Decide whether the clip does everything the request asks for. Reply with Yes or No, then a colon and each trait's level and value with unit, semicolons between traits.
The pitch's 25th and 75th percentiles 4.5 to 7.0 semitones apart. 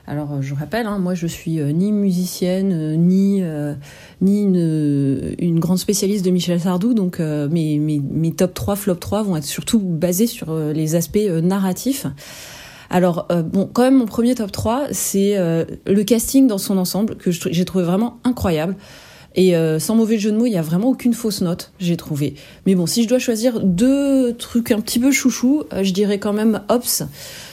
Yes: average, 5.0 semitones